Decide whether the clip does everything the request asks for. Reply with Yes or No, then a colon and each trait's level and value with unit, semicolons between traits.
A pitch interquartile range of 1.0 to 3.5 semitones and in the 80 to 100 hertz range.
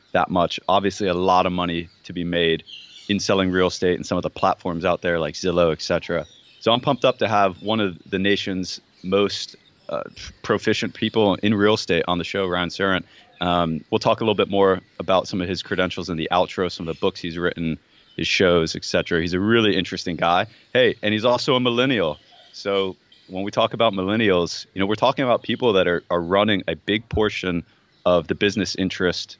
Yes: average, 2.7 semitones; very low, 95 Hz